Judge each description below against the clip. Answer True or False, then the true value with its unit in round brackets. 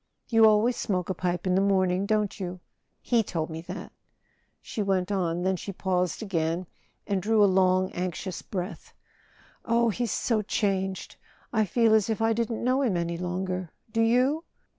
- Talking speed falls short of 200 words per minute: True (170 wpm)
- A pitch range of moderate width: True (3.4 semitones)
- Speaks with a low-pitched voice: False (195 Hz)